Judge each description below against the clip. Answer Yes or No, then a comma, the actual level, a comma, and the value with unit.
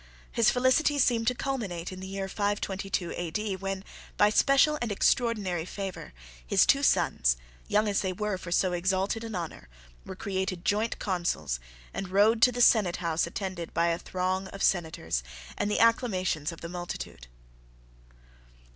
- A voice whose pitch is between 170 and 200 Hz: Yes, high, 190 Hz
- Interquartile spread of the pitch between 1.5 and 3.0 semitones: No, average, 3.5 semitones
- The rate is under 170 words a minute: Yes, average, 160 wpm